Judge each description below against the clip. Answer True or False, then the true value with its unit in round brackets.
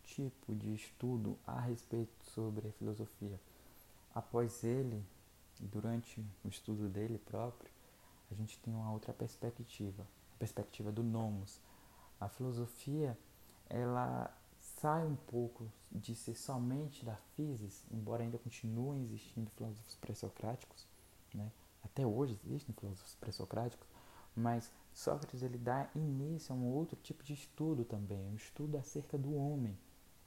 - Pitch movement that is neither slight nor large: True (3.1 semitones)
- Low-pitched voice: True (115 Hz)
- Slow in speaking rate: False (130 wpm)